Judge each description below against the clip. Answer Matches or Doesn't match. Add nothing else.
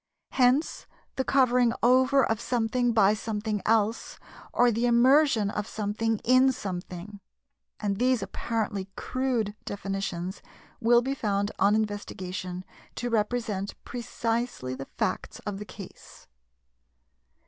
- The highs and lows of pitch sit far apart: Doesn't match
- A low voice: Doesn't match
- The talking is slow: Matches